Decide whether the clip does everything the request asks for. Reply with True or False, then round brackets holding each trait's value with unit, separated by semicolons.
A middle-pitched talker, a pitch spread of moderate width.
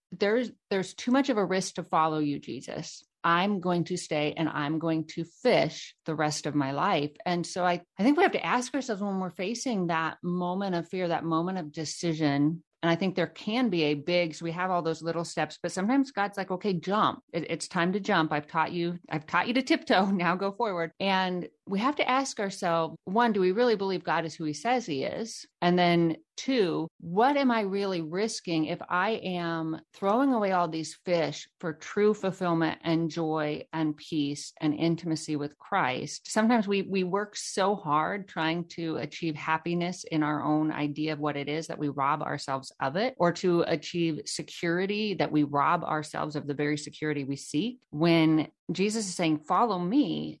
True (170 Hz; 3.7 semitones)